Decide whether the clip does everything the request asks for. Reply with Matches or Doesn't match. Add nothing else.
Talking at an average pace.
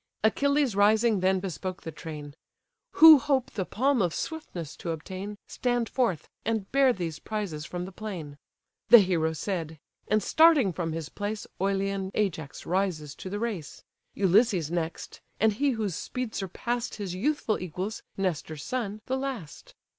Matches